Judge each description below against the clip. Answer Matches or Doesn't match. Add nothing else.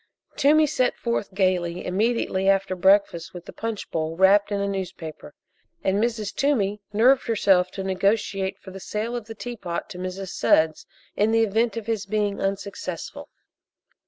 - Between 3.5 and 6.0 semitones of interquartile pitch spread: Doesn't match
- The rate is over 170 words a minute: Doesn't match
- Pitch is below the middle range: Doesn't match